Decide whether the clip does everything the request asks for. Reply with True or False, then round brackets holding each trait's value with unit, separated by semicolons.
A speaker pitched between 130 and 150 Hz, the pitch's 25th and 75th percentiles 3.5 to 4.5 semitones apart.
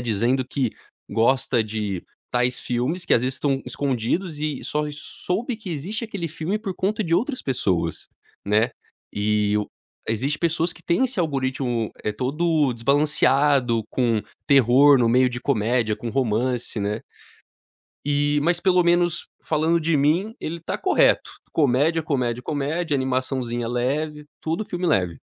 False (135 Hz; 5.3 semitones)